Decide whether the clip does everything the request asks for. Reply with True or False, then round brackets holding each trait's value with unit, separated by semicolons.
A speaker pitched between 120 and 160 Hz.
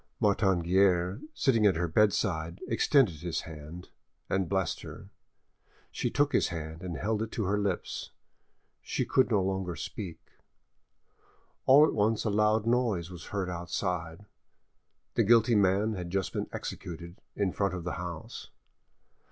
False (95 Hz)